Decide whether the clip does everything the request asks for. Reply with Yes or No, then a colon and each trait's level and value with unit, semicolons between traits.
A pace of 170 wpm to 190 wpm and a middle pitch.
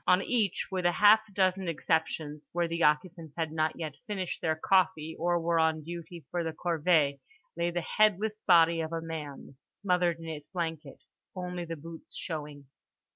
Yes: average, 175 wpm; medium, 165 Hz